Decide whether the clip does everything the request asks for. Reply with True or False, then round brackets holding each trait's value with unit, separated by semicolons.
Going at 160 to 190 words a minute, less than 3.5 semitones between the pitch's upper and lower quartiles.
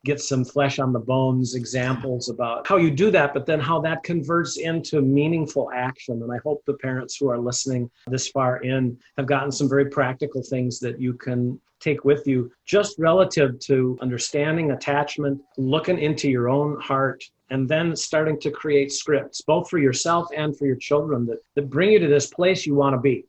False (200 wpm; 2.8 semitones)